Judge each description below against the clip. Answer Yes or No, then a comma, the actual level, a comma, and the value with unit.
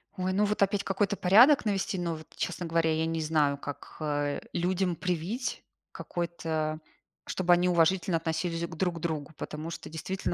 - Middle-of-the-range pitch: Yes, medium, 170 Hz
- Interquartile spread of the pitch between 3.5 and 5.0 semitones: No, average, 2.8 semitones